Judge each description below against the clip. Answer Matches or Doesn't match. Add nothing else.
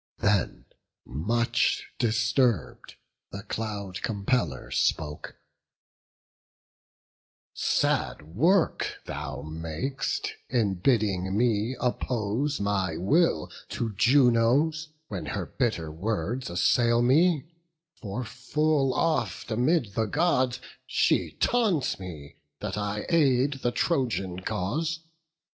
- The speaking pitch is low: Matches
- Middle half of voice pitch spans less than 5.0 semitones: Doesn't match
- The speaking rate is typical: Doesn't match